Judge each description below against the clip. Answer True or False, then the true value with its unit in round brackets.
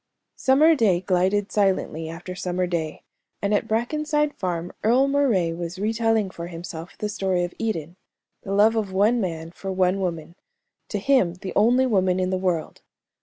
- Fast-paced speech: False (170 wpm)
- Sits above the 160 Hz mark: True (190 Hz)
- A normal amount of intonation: True (4.0 semitones)